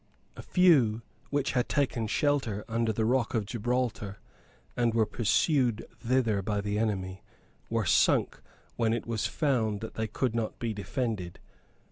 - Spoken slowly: No, average, 150 wpm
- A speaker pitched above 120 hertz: No, low, 115 Hz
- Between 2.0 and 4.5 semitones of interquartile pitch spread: Yes, average, 2.9 semitones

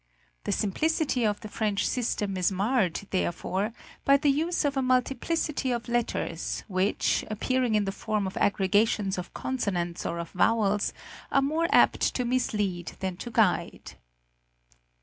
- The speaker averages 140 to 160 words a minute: Yes, average, 150 wpm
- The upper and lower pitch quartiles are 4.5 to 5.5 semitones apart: Yes, average, 5.0 semitones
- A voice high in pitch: Yes, high, 215 Hz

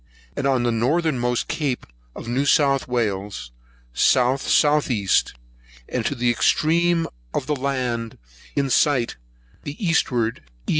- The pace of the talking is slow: Yes, slow, 115 wpm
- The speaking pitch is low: Yes, low, 130 Hz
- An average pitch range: Yes, average, 3.7 semitones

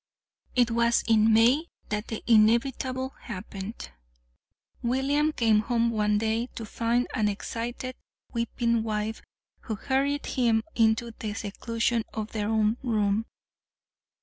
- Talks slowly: Yes, slow, 120 wpm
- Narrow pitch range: Yes, narrow, 1.9 semitones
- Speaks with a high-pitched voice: Yes, high, 230 Hz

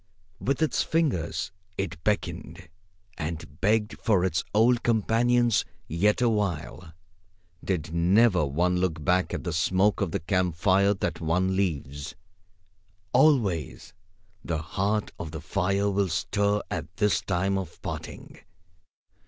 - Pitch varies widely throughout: No, average, 4.0 semitones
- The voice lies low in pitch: Yes, very low, 95 Hz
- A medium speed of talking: No, slow, 130 wpm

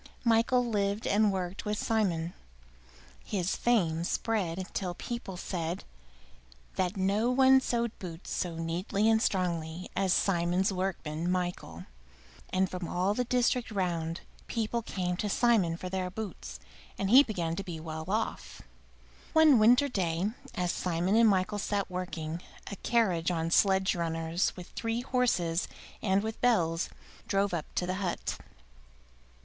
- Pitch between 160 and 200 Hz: Yes, high, 190 Hz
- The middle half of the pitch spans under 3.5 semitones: No, average, 4.2 semitones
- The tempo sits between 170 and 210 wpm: No, average, 145 wpm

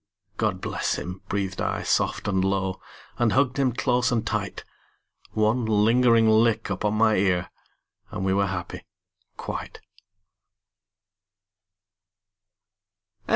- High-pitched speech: No, low, 110 Hz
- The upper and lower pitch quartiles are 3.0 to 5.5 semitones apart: Yes, average, 3.5 semitones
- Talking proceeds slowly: Yes, slow, 110 wpm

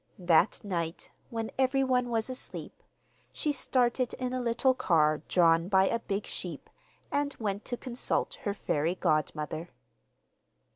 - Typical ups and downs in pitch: No, wide, 6.8 semitones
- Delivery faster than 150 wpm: No, slow, 135 wpm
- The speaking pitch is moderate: No, high, 220 Hz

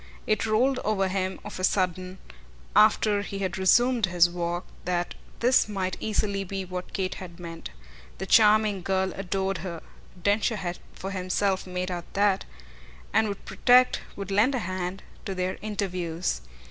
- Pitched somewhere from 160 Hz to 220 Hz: Yes, high, 190 Hz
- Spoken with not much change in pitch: Yes, narrow, 2.3 semitones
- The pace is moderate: Yes, average, 160 wpm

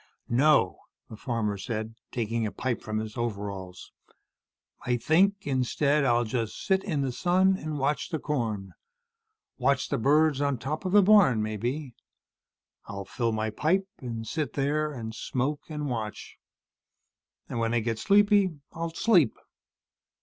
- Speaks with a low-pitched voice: Yes, low, 130 Hz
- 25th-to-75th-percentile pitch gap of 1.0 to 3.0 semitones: No, wide, 5.6 semitones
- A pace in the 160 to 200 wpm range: No, average, 150 wpm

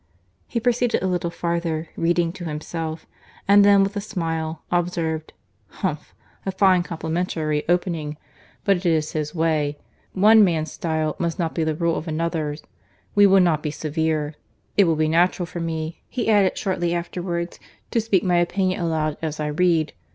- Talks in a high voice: No, medium, 170 Hz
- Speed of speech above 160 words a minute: Yes, average, 170 wpm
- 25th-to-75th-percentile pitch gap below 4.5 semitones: Yes, narrow, 2.5 semitones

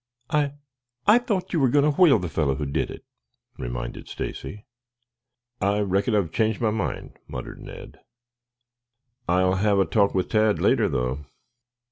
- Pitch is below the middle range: Yes, low, 100 Hz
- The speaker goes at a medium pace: Yes, average, 155 wpm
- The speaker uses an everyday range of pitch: No, wide, 6.9 semitones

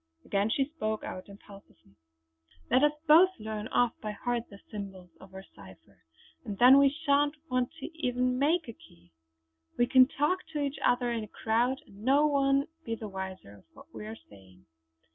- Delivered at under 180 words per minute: No, average, 185 wpm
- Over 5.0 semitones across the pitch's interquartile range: Yes, wide, 5.6 semitones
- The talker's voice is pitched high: Yes, high, 240 Hz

